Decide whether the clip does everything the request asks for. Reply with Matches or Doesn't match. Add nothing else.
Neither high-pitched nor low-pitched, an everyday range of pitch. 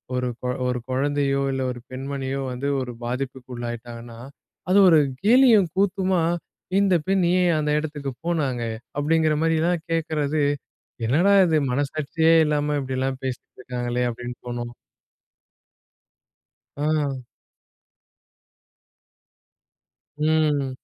Matches